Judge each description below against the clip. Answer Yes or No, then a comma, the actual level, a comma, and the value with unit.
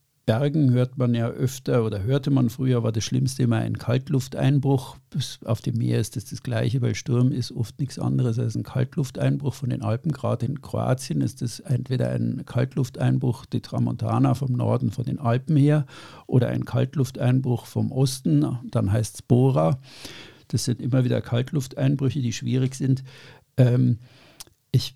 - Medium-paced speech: Yes, average, 170 wpm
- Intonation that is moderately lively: No, narrow, 2.1 semitones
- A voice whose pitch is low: Yes, low, 130 Hz